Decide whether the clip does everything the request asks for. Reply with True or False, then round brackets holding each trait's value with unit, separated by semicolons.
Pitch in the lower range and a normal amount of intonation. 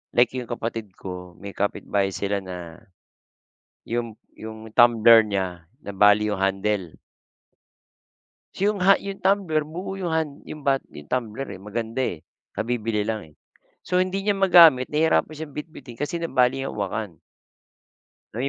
False (115 Hz; 7.2 semitones)